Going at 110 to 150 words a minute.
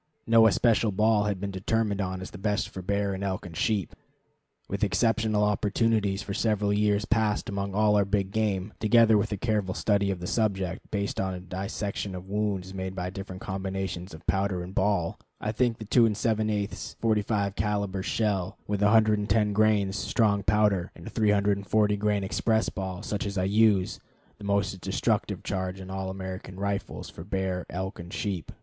No: average, 180 wpm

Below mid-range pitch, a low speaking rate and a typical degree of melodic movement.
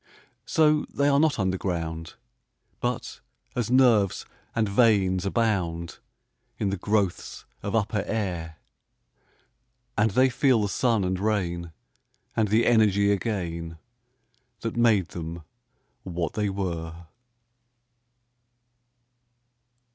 Yes: low, 100 Hz; slow, 100 wpm; average, 4.6 semitones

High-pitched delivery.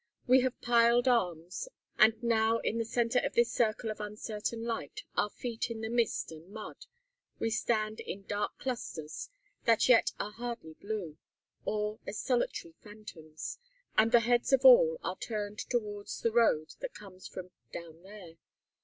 Yes: high, 220 Hz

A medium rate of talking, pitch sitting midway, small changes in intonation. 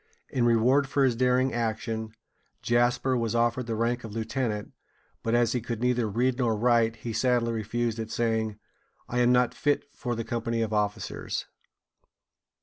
No: average, 165 wpm; low, 115 Hz; narrow, 1.6 semitones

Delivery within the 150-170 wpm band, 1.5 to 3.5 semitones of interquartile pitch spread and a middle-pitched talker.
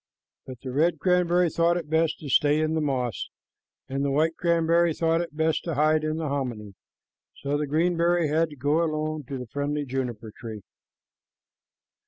No: average, 185 wpm; average, 3.1 semitones; medium, 155 Hz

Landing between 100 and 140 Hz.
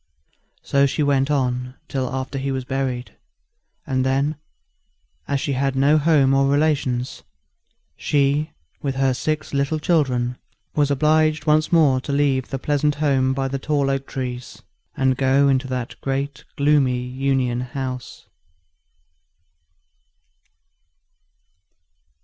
Yes: low, 135 Hz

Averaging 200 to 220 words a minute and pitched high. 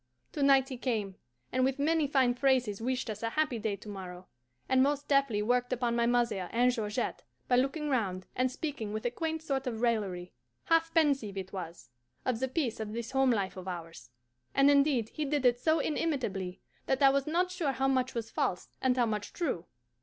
Yes: fast, 205 wpm; very high, 250 Hz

